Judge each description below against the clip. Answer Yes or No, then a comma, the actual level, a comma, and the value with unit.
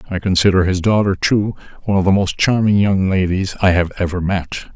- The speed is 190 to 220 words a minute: Yes, average, 200 wpm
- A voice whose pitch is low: Yes, very low, 95 Hz